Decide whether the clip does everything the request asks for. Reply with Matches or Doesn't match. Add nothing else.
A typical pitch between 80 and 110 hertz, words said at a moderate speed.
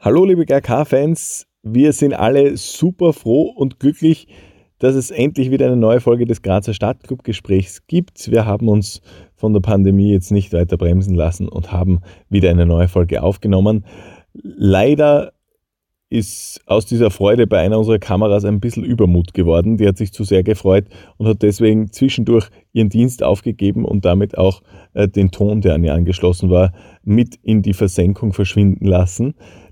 Matches